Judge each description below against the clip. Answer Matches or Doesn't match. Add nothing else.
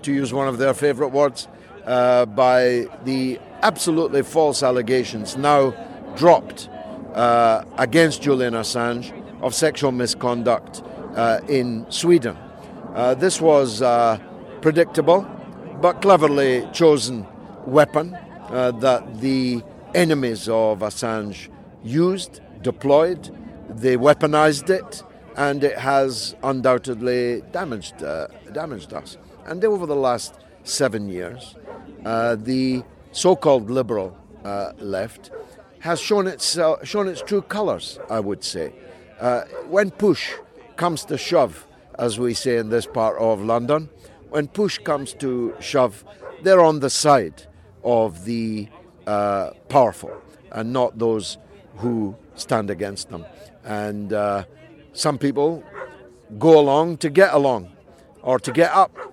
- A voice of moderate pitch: Doesn't match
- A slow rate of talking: Matches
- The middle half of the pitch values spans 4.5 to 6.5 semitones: Matches